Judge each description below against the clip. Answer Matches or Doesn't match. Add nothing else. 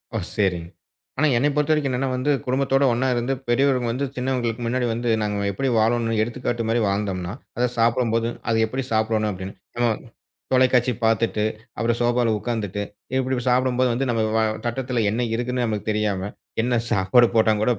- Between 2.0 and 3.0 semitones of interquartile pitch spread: Matches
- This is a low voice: Matches